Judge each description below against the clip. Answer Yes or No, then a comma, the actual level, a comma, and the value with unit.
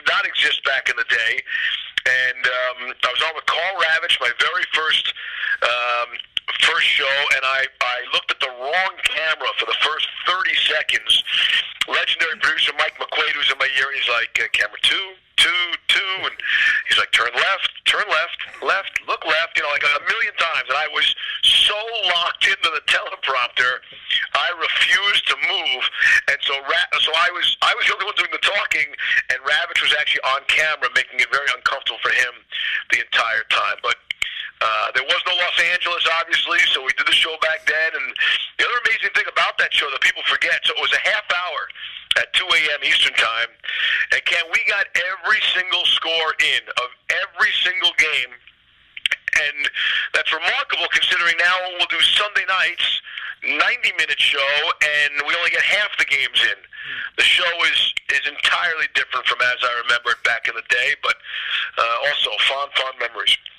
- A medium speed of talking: Yes, average, 180 wpm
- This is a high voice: Yes, high, 195 Hz